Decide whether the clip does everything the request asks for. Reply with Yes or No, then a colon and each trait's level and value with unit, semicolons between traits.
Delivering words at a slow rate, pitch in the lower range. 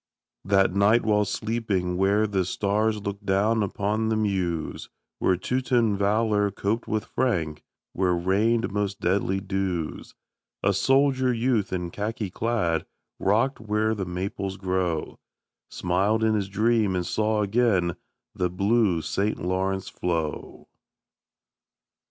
Yes: slow, 125 wpm; low, 100 Hz